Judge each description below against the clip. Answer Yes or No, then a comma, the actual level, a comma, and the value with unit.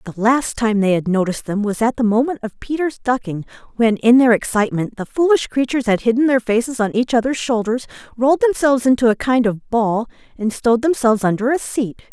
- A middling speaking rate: No, fast, 210 wpm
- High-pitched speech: Yes, high, 235 Hz